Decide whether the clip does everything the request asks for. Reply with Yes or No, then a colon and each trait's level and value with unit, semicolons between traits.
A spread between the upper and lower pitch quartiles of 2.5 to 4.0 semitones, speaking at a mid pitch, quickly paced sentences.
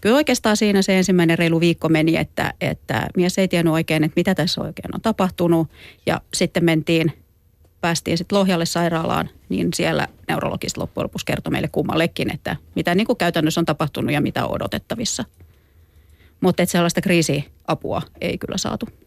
Yes: average, 2.9 semitones; medium, 170 Hz; fast, 165 wpm